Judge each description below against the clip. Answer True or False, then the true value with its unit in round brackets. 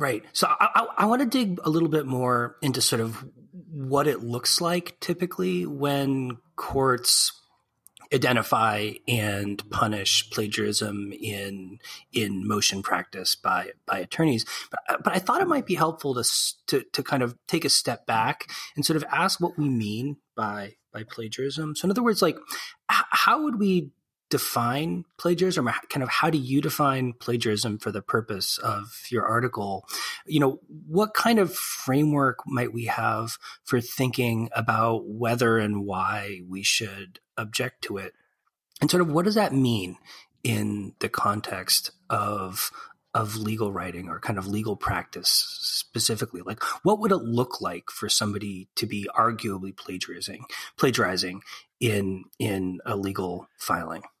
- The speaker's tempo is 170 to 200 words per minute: False (155 wpm)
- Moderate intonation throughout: False (6.5 semitones)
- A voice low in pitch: True (120 Hz)